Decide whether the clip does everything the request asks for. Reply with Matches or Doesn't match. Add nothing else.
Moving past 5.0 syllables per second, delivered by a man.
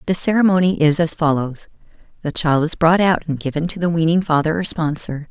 Doesn't match